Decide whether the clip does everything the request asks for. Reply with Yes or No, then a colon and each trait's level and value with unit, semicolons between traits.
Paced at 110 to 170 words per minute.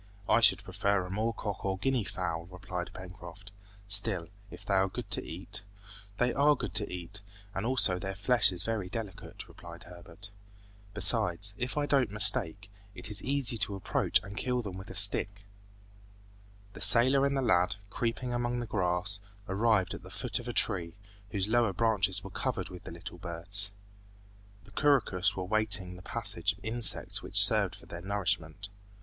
No: average, 180 wpm